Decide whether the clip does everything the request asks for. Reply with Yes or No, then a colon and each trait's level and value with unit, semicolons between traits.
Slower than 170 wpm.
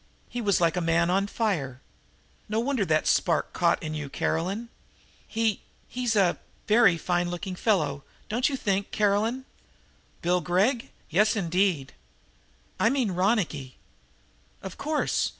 Yes: average, 140 wpm